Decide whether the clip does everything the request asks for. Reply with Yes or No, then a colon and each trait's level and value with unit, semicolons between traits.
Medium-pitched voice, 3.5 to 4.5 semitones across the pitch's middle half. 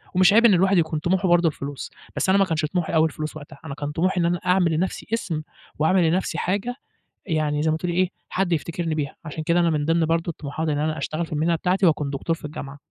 No: medium, 165 Hz; average, 2.8 semitones